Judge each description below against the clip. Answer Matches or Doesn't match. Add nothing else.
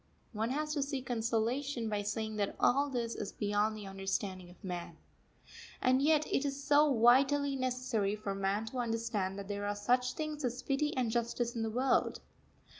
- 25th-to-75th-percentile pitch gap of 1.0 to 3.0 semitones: Doesn't match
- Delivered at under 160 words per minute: Doesn't match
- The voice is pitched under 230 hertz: Doesn't match